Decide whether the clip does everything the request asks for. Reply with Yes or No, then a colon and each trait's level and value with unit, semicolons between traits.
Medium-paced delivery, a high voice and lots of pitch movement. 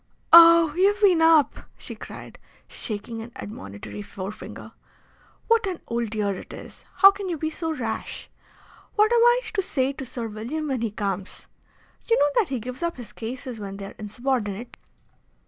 Yes: average, 175 wpm; very high, 260 Hz; wide, 7.8 semitones